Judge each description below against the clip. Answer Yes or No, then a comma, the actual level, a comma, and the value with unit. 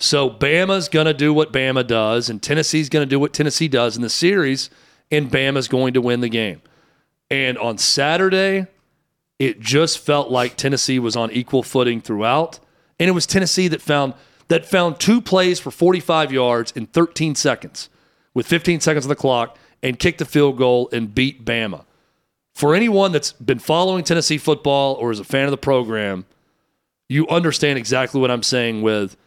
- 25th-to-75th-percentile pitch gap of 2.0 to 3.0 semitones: No, average, 4.6 semitones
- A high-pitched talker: No, medium, 140 Hz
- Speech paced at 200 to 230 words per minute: No, average, 185 wpm